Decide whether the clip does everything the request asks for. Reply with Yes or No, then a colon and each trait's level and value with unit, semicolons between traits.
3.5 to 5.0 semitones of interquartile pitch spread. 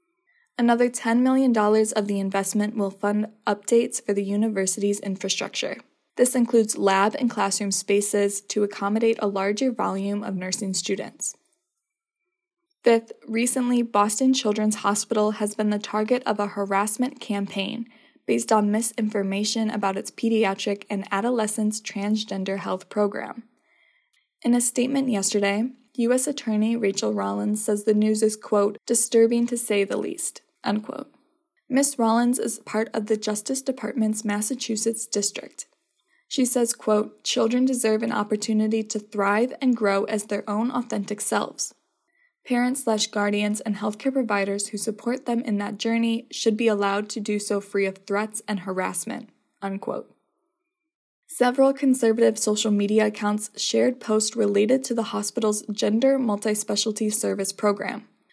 No: average, 3.0 semitones